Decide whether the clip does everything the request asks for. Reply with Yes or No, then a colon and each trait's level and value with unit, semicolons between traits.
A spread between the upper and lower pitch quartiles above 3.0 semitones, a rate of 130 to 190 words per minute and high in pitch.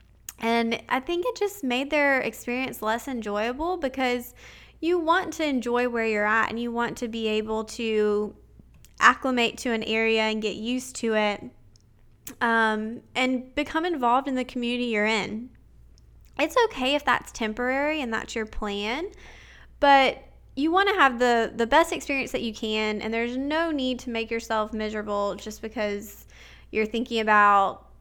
Yes: average, 3.5 semitones; average, 165 wpm; high, 235 Hz